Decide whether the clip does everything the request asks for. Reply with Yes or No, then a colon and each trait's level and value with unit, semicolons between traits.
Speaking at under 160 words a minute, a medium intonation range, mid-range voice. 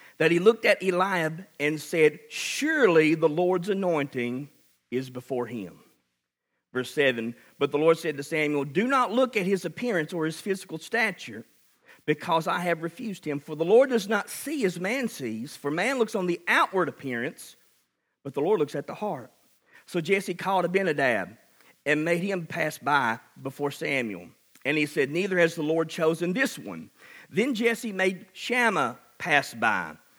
No: average, 175 wpm; average, 4.9 semitones; medium, 170 Hz